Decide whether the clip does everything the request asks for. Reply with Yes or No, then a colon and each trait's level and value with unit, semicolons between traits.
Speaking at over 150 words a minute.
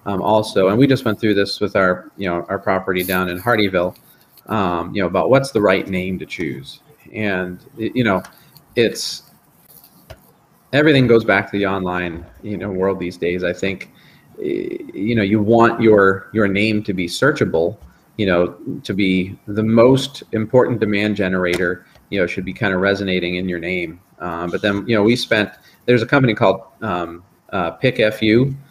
Yes: average, 180 wpm